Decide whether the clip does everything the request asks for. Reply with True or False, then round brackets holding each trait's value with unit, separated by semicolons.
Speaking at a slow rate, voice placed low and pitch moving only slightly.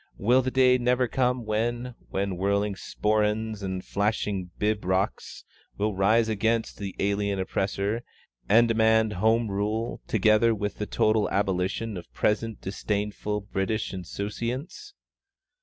True (125 wpm; 105 Hz; 2.3 semitones)